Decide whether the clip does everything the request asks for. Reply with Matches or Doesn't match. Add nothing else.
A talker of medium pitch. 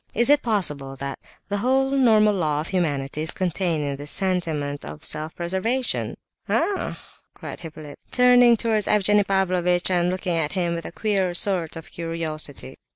Matches